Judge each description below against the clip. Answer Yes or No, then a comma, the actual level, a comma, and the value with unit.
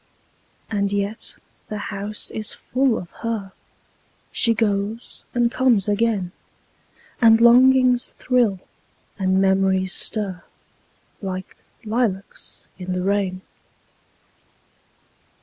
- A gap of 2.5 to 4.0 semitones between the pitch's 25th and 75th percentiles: Yes, average, 3.3 semitones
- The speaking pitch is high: Yes, high, 205 Hz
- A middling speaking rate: No, slow, 95 wpm